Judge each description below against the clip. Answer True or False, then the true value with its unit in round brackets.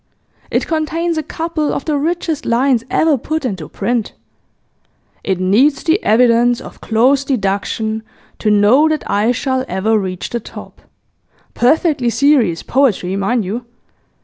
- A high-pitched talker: True (245 Hz)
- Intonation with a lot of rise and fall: True (5.7 semitones)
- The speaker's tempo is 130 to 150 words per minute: True (140 wpm)